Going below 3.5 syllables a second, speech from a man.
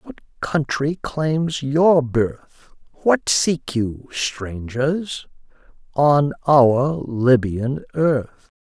Yes: 2.2 syllables/s; male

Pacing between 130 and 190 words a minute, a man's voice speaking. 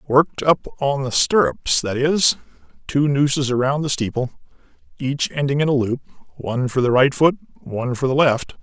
Yes: average, 175 wpm; male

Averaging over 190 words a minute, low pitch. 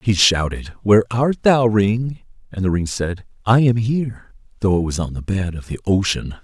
Yes: fast, 205 wpm; low, 105 Hz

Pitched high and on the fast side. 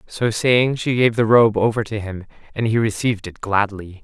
No: low, 110 Hz; fast, 210 wpm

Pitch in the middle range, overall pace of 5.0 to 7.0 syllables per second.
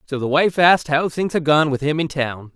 Yes: medium, 150 Hz; 5.5 syllables/s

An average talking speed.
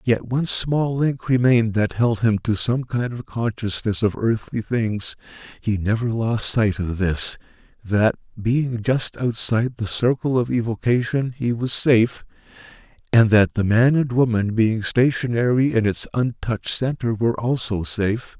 Yes: average, 155 wpm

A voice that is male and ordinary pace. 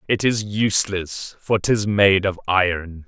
Yes: male; average, 155 wpm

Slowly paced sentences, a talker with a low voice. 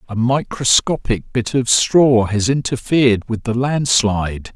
Yes: slow, 130 wpm; low, 120 Hz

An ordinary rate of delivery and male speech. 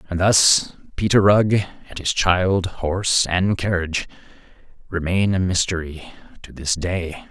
No: slow, 130 wpm; male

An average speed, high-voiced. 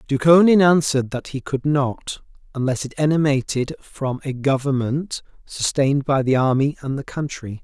No: average, 150 wpm; medium, 140 Hz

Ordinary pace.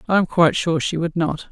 No: fast, 275 wpm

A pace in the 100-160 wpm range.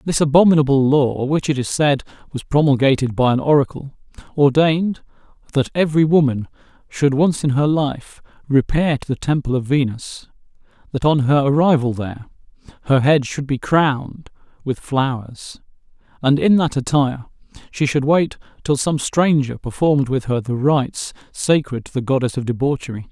Yes: average, 155 wpm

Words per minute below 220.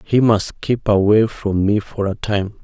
Yes: fast, 205 wpm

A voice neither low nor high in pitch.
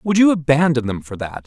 Yes: medium, 145 Hz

